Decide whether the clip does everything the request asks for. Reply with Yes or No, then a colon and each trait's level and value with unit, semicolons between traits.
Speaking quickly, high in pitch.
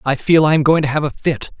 No: fast, 340 wpm; medium, 150 Hz